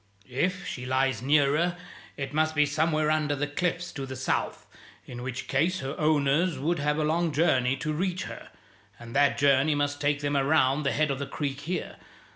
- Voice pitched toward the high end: No, medium, 145 Hz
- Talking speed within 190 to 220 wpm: Yes, average, 195 wpm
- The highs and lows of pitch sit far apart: No, narrow, 2.4 semitones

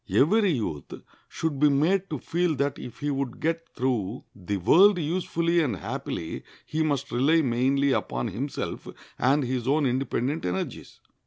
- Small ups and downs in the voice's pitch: No, average, 4.7 semitones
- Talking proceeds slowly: No, average, 155 wpm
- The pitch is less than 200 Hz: Yes, medium, 140 Hz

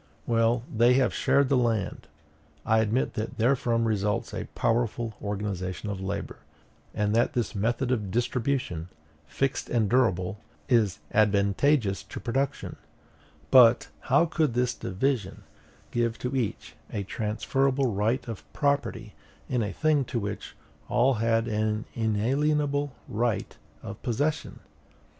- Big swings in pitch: No, average, 3.7 semitones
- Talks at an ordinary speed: No, slow, 130 wpm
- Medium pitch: No, low, 115 Hz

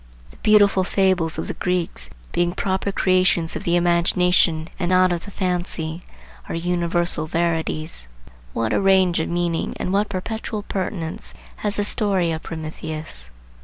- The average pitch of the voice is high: No, medium, 175 Hz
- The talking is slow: No, average, 150 wpm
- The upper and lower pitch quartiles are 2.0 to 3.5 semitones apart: Yes, narrow, 2.4 semitones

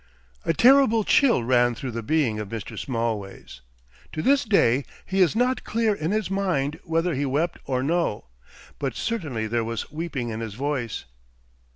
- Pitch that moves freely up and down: Yes, wide, 8.7 semitones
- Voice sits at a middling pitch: Yes, medium, 145 Hz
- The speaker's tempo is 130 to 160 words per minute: No, average, 170 wpm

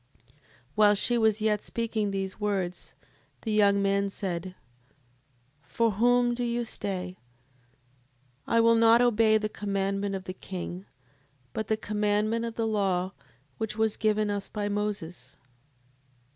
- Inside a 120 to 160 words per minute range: Yes, average, 140 wpm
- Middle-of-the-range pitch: No, high, 210 Hz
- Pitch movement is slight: Yes, narrow, 2.2 semitones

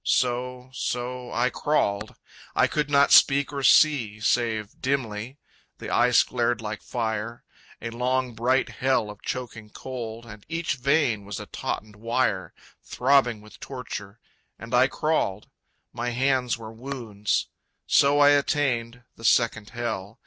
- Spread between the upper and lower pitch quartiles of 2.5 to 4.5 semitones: Yes, average, 3.1 semitones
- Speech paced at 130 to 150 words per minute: Yes, average, 140 wpm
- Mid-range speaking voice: No, low, 120 Hz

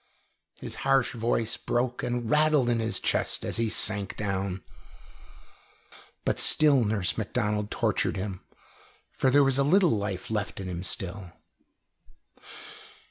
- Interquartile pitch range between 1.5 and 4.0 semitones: No, average, 4.6 semitones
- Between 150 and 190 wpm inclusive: No, slow, 135 wpm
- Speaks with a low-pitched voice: Yes, low, 110 Hz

